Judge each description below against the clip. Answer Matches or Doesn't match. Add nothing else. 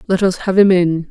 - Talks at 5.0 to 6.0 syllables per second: Matches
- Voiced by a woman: Matches